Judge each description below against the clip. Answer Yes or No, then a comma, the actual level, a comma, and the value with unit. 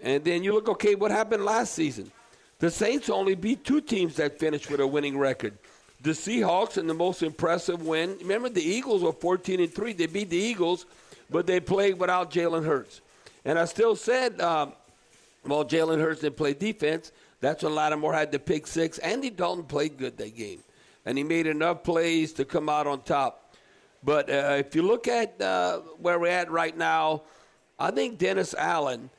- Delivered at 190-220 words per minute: Yes, average, 195 wpm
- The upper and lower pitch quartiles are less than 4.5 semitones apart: No, average, 5.0 semitones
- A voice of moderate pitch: Yes, medium, 170 Hz